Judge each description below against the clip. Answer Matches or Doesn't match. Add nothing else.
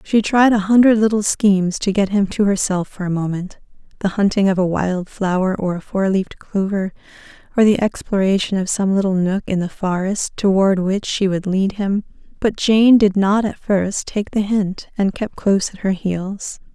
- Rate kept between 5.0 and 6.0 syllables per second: Doesn't match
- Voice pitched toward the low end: Doesn't match